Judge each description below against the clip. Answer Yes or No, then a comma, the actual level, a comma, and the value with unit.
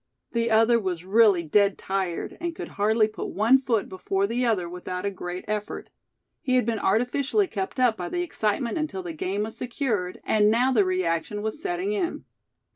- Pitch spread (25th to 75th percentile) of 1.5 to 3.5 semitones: No, average, 4.7 semitones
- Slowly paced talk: No, average, 190 wpm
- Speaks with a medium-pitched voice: No, high, 215 Hz